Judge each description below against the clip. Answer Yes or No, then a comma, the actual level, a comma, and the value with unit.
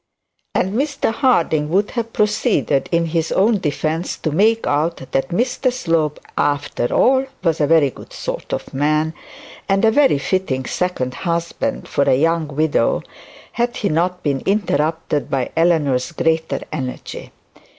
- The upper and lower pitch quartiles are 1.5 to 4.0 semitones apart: No, wide, 5.6 semitones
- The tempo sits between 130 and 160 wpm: Yes, average, 150 wpm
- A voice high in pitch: No, medium, 165 Hz